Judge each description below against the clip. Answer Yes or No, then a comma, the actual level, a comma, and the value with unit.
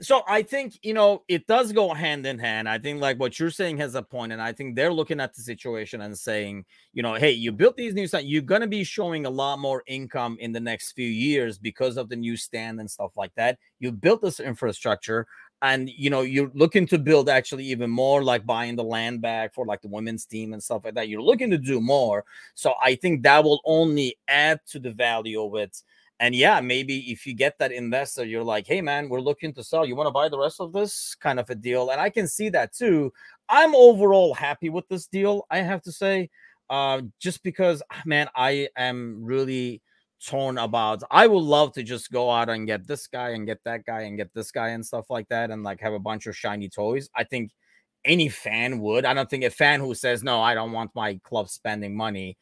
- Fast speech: Yes, fast, 240 wpm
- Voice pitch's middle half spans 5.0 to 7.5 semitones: Yes, wide, 5.4 semitones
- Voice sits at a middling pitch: No, low, 130 Hz